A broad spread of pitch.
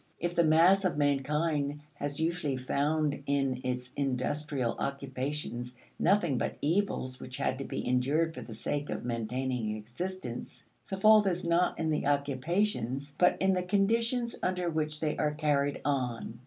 No: average, 4.7 semitones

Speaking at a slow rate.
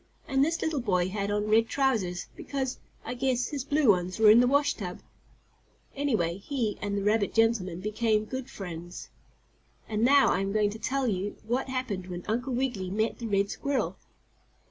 No: average, 180 wpm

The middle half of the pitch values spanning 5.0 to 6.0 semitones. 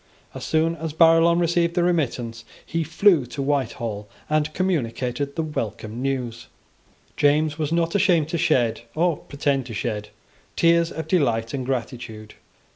Yes: wide, 5.5 semitones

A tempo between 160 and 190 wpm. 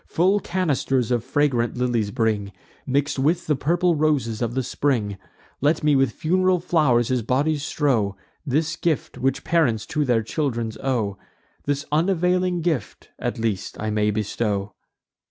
No: average, 150 wpm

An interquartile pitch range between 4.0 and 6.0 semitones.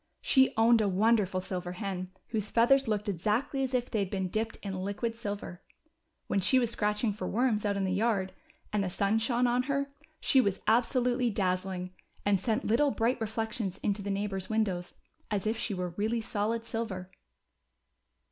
No: average, 3.2 semitones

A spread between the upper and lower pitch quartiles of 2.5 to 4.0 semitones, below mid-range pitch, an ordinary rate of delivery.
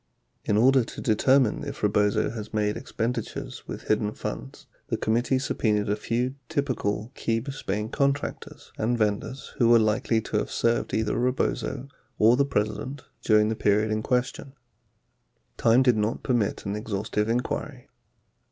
Yes: average, 3.0 semitones; low, 115 Hz; average, 150 wpm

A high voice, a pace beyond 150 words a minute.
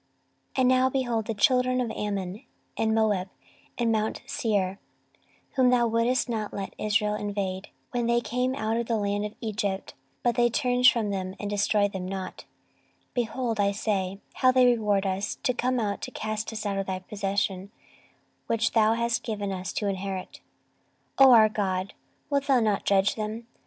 Yes: high, 215 Hz; average, 180 wpm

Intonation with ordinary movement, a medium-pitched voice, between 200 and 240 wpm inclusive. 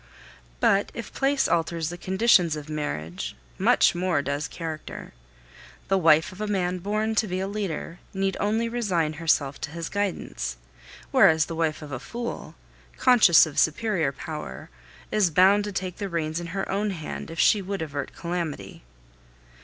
No: average, 4.4 semitones; medium, 175 Hz; average, 165 wpm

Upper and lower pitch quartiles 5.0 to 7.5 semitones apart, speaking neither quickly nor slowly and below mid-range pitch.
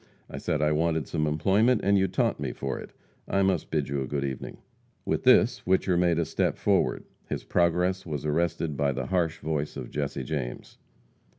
No: average, 3.7 semitones; average, 190 wpm; very low, 80 Hz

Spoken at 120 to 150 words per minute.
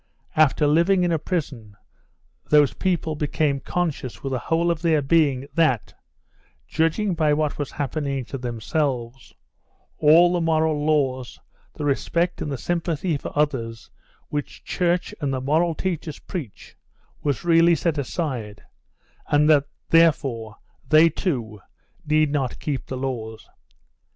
Yes: slow, 135 wpm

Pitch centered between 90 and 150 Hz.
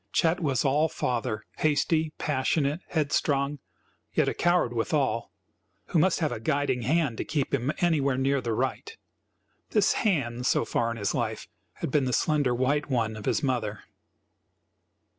Yes: medium, 140 Hz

